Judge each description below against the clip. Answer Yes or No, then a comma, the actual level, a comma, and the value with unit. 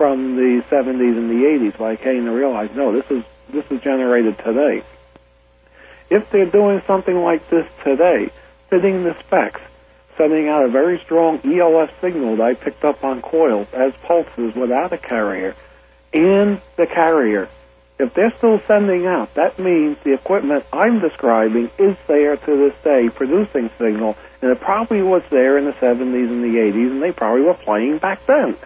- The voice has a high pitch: No, low, 135 Hz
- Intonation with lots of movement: Yes, wide, 6.7 semitones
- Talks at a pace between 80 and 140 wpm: No, average, 175 wpm